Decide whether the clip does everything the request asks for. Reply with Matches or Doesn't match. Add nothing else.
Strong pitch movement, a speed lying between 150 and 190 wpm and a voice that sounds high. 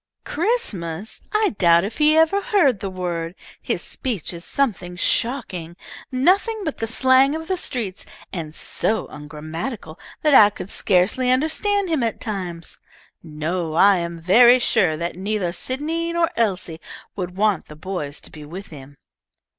Matches